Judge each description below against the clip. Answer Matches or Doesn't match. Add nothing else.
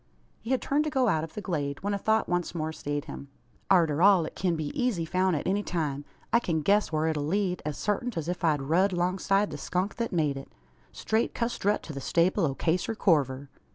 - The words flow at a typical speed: Doesn't match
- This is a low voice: Doesn't match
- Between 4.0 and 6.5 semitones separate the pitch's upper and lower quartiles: Matches